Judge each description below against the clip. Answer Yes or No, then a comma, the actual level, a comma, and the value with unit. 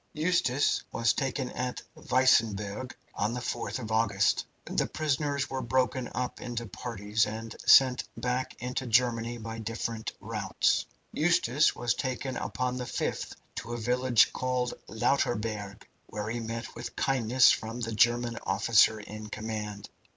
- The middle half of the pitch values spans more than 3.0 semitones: No, narrow, 2.5 semitones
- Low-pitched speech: Yes, low, 120 Hz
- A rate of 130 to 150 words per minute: Yes, average, 140 wpm